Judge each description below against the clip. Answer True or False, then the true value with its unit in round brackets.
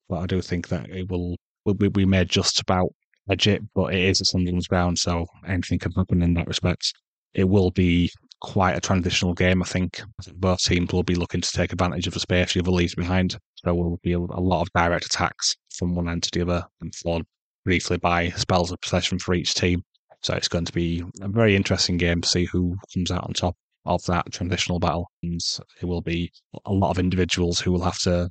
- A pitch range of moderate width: False (1.3 semitones)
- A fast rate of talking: True (230 wpm)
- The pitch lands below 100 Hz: True (90 Hz)